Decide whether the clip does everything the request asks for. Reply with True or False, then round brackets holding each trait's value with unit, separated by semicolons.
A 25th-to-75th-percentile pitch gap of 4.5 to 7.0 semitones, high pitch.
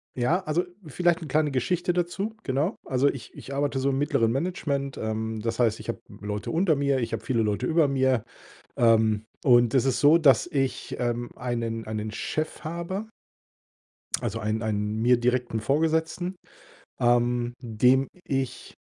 False (5.1 semitones; 130 Hz)